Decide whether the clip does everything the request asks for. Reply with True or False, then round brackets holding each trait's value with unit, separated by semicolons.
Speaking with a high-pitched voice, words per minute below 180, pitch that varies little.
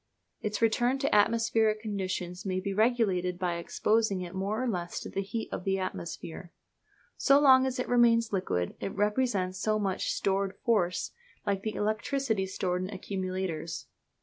False (200 Hz; 160 wpm; 3.6 semitones)